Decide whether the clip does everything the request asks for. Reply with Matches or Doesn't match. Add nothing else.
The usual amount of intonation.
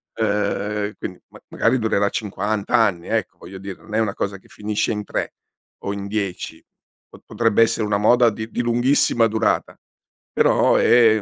Doesn't match